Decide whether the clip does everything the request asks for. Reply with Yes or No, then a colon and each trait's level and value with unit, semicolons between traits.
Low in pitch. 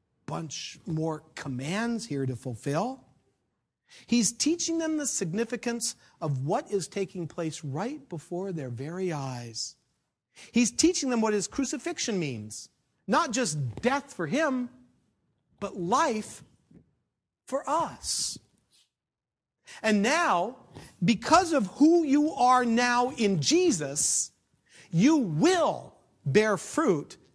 No: high, 225 Hz